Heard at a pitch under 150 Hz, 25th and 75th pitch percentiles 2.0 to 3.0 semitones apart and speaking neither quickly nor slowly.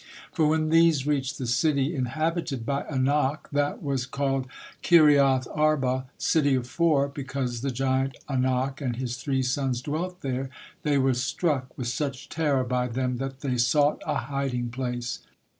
Yes: low, 135 Hz; narrow, 2.4 semitones; average, 160 wpm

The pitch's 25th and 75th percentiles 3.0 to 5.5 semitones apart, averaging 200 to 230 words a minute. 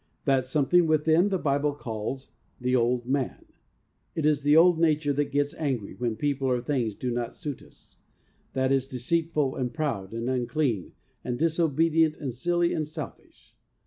No: average, 3.9 semitones; average, 175 wpm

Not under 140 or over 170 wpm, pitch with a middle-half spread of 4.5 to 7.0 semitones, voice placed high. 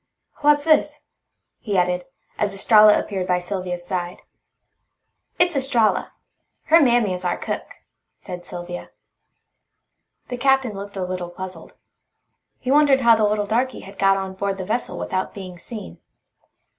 Yes: average, 145 wpm; average, 5.1 semitones; high, 200 Hz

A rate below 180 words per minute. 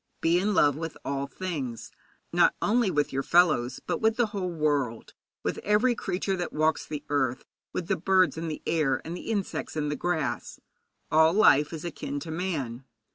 No: average, 185 wpm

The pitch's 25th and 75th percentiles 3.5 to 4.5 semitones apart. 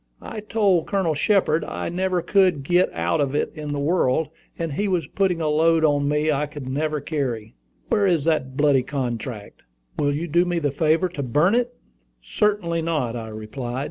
Yes: average, 4.2 semitones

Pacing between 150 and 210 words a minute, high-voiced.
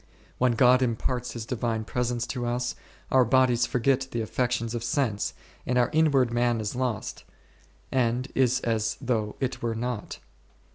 No: average, 160 wpm; low, 120 Hz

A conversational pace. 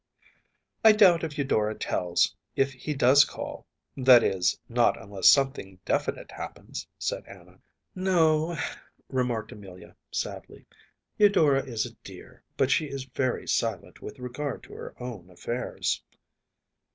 No: slow, 130 wpm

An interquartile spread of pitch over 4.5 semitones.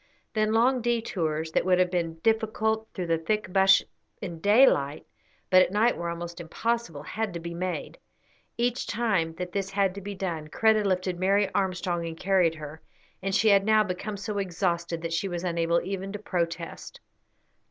No: average, 3.8 semitones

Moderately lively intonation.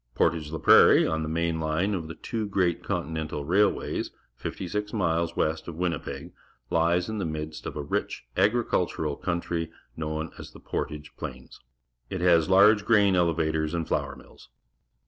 Yes: average, 3.1 semitones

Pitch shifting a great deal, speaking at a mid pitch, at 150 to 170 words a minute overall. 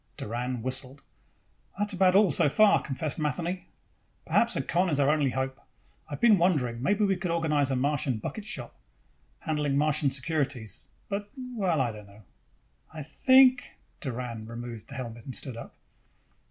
Yes: wide, 5.9 semitones; medium, 145 Hz; average, 165 wpm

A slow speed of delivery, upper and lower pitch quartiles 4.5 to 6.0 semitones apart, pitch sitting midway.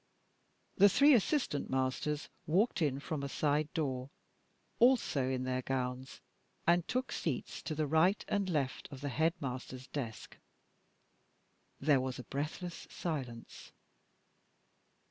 Yes: slow, 125 wpm; average, 4.8 semitones; medium, 145 Hz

